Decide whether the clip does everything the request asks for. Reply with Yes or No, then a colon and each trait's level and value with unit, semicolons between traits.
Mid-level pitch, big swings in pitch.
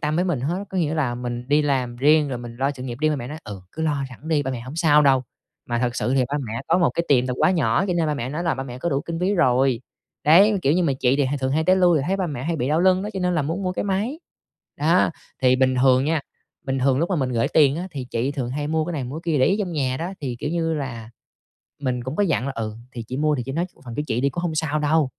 No: medium, 145 Hz; average, 4.4 semitones